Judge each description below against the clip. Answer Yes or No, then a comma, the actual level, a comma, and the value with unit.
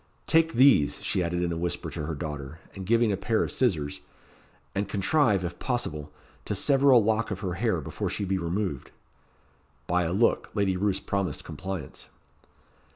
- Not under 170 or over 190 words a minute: Yes, average, 175 wpm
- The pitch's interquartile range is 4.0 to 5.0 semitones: Yes, average, 4.7 semitones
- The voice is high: No, very low, 95 Hz